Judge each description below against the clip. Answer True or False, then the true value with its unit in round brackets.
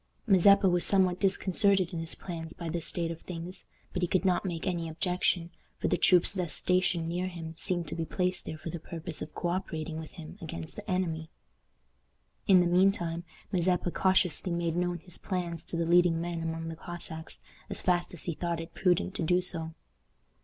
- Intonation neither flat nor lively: False (1.7 semitones)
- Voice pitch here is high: False (175 Hz)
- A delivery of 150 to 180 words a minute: False (205 wpm)